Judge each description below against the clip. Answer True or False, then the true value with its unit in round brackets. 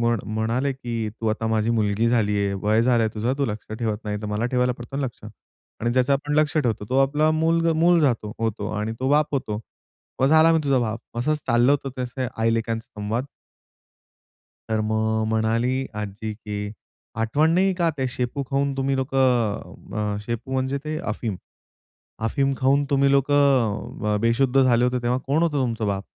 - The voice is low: True (120 Hz)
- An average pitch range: True (3.8 semitones)